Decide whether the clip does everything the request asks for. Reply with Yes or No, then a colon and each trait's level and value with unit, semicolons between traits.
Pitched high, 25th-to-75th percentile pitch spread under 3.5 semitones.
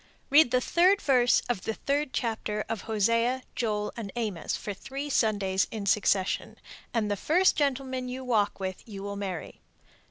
No: high, 230 Hz; average, 4.3 semitones